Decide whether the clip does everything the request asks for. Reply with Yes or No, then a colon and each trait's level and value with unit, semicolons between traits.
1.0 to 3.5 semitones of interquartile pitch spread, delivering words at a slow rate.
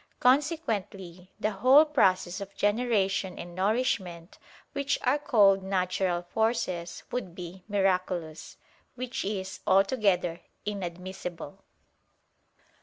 No: average, 3.9 semitones; slow, 95 wpm